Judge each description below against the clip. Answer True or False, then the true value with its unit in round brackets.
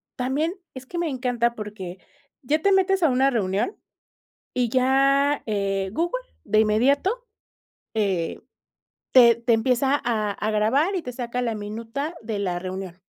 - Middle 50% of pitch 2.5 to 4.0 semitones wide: False (4.8 semitones)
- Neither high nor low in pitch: False (240 Hz)